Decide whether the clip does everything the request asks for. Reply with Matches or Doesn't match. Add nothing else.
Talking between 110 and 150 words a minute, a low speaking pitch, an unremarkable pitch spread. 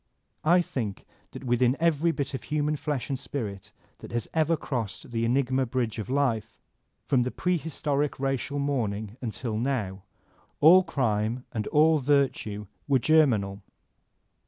Matches